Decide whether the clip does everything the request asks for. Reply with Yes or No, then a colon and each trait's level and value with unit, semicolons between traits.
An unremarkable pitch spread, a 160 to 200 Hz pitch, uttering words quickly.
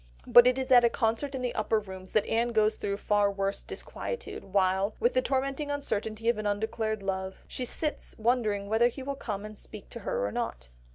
No: average, 3.6 semitones; high, 220 Hz; fast, 215 wpm